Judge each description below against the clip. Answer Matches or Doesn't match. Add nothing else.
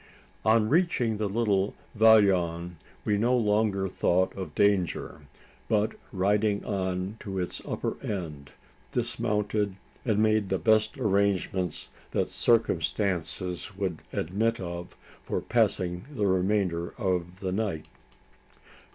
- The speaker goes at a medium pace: Doesn't match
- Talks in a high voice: Doesn't match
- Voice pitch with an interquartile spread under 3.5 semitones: Matches